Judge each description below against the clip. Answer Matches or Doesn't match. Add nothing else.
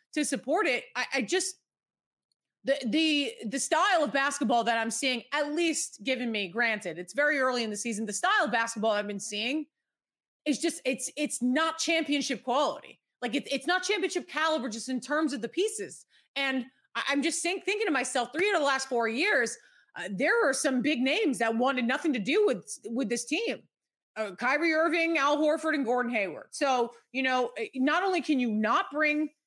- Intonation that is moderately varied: Matches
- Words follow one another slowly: Doesn't match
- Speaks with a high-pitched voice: Matches